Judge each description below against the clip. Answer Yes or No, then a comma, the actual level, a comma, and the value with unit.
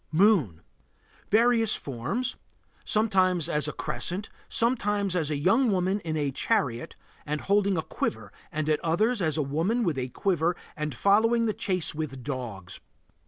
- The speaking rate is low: No, average, 155 wpm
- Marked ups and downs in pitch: Yes, wide, 5.8 semitones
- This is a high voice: No, medium, 175 Hz